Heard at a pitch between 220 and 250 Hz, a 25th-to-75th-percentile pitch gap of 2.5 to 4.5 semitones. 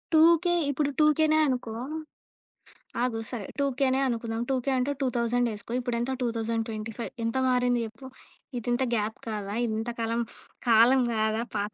Yes: high, 240 Hz; average, 2.8 semitones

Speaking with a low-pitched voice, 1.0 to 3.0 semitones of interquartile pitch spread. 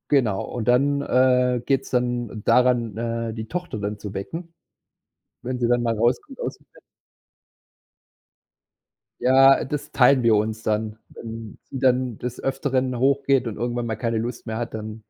Yes: low, 120 Hz; narrow, 2.6 semitones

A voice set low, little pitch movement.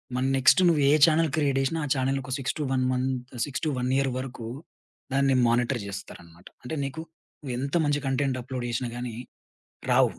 Yes: low, 130 Hz; narrow, 2.1 semitones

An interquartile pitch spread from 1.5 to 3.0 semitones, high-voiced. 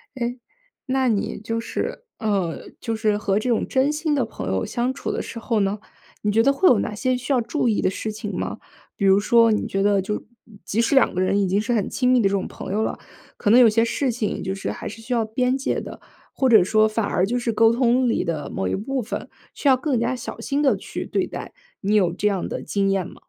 No: average, 3.7 semitones; high, 225 Hz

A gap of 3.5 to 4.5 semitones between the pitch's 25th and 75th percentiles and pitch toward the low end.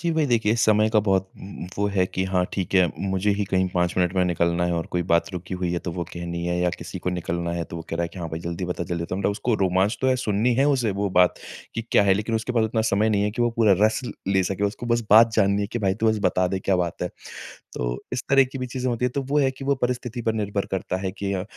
Yes: average, 4.2 semitones; low, 100 Hz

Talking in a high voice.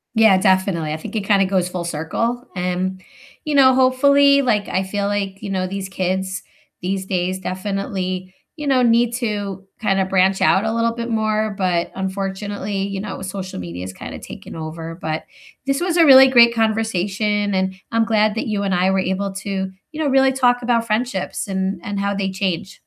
Yes: high, 195 Hz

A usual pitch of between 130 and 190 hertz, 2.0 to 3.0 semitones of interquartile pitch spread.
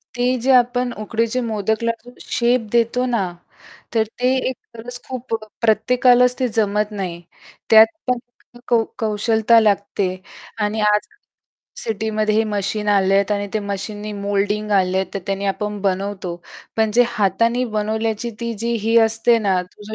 No: high, 220 Hz; narrow, 2.6 semitones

